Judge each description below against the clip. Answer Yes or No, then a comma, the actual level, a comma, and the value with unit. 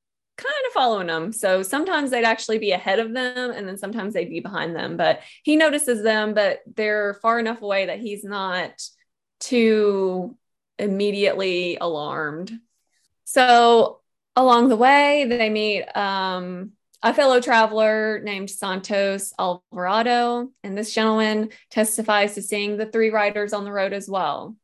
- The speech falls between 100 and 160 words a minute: Yes, average, 150 wpm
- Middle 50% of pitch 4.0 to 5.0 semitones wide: No, average, 3.2 semitones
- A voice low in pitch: No, high, 215 Hz